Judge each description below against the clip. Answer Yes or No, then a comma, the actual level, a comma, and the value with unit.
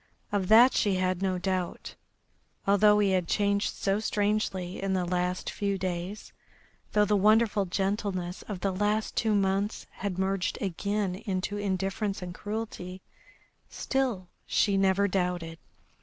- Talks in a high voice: Yes, high, 195 Hz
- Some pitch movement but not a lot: No, narrow, 2.0 semitones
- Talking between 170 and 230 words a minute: No, average, 140 wpm